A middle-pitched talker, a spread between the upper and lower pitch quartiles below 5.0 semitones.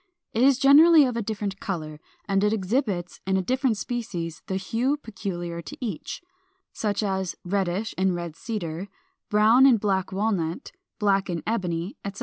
No: high, 200 Hz; average, 4.2 semitones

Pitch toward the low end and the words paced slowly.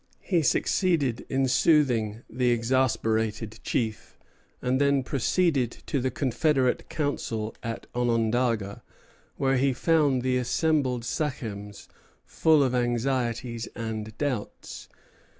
Yes: low, 125 Hz; slow, 105 wpm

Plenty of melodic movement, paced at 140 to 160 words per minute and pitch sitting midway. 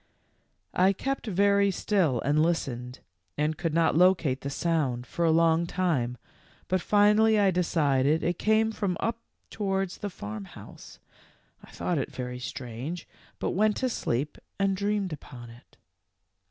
Yes: wide, 6.4 semitones; average, 150 wpm; medium, 170 Hz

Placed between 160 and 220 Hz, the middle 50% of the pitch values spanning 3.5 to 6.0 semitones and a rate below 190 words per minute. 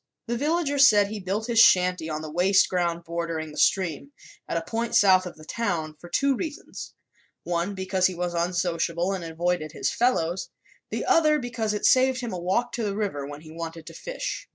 No: medium, 185 Hz; wide, 5.5 semitones; average, 200 wpm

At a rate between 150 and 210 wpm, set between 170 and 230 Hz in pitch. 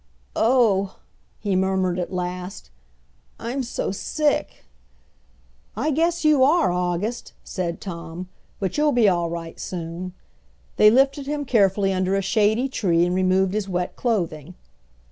No: slow, 135 wpm; high, 190 Hz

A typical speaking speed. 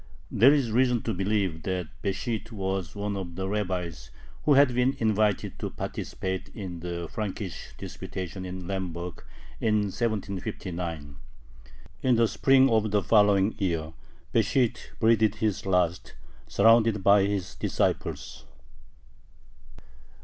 No: slow, 120 wpm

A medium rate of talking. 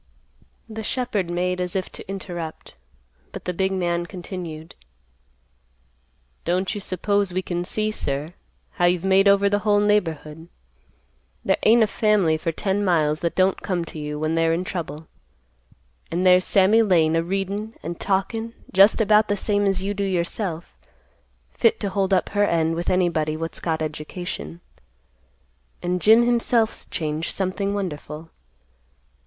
Yes: average, 155 wpm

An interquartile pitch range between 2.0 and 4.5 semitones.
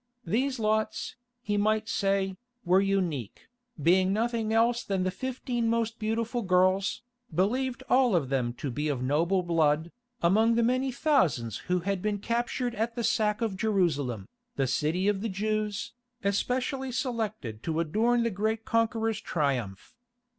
No: average, 5.0 semitones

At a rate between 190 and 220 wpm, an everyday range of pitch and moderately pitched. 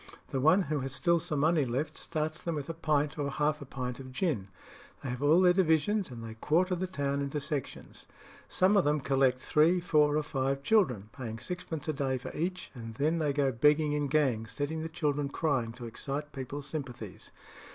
Yes: fast, 205 wpm; average, 3.1 semitones; medium, 145 Hz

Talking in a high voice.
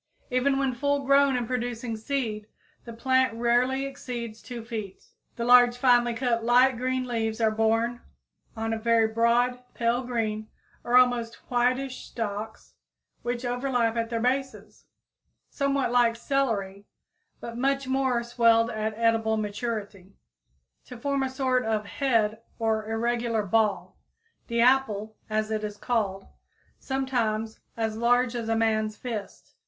Yes: high, 235 Hz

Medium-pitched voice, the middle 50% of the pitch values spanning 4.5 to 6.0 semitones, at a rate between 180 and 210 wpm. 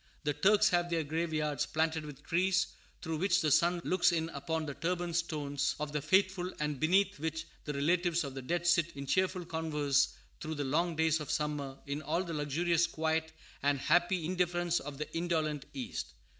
No: medium, 160 Hz; average, 2.7 semitones; average, 185 wpm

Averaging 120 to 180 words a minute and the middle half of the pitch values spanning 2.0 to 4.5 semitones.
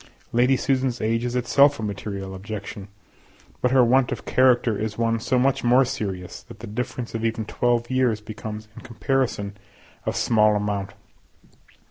Yes: average, 160 wpm; average, 2.9 semitones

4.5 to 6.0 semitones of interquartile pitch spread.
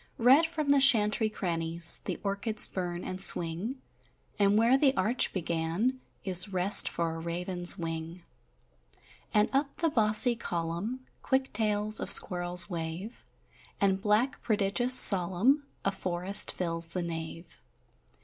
Yes: average, 5.1 semitones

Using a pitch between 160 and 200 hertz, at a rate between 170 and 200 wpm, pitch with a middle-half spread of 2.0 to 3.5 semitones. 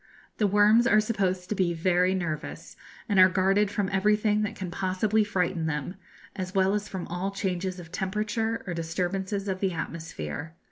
Yes: high, 190 Hz; average, 175 wpm; narrow, 2.6 semitones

